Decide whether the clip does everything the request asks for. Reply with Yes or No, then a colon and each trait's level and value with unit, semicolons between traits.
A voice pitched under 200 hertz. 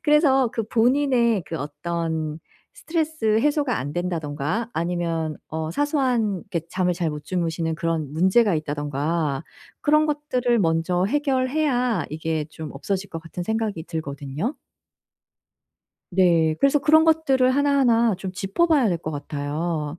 Yes: medium, 185 Hz